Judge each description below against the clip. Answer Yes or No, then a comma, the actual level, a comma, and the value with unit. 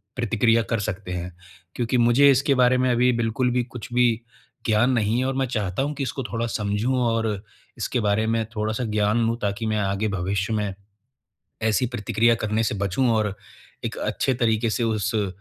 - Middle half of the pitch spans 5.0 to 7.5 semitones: No, average, 2.7 semitones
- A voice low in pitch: Yes, low, 115 Hz